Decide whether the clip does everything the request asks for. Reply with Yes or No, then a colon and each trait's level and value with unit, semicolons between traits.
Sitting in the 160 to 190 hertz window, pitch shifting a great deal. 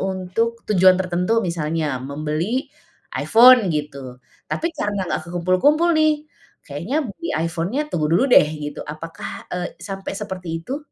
Yes: medium, 185 Hz; wide, 6.1 semitones